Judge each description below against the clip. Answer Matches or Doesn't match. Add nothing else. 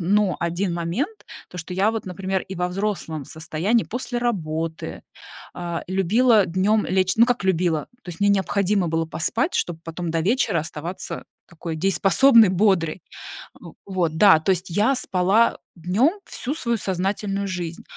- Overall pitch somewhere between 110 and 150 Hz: Doesn't match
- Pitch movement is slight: Doesn't match